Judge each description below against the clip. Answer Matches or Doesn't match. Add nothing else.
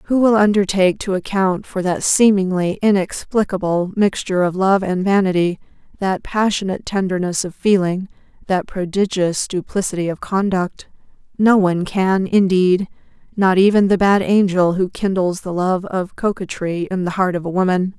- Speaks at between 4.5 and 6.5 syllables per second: Matches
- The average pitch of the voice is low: Doesn't match